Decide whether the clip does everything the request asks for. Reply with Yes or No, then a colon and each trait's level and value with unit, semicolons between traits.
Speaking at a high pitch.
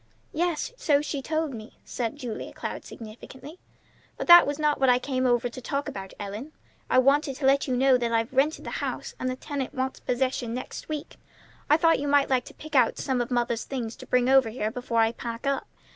Yes: very high, 260 Hz